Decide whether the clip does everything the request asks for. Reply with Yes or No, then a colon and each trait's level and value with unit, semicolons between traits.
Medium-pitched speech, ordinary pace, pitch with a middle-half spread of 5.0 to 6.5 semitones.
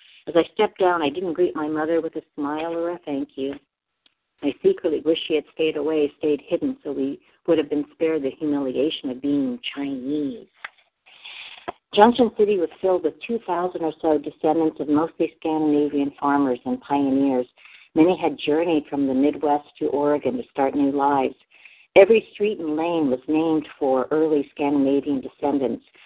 No: medium, 155 Hz; average, 170 wpm; average, 2.7 semitones